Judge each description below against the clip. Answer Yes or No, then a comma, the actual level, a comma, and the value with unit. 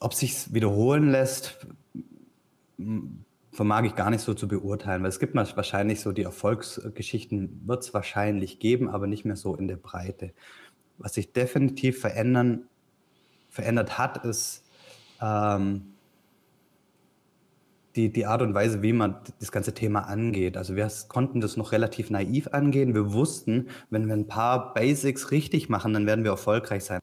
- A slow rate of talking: No, average, 160 wpm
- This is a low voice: Yes, low, 110 Hz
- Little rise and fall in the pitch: No, average, 3.3 semitones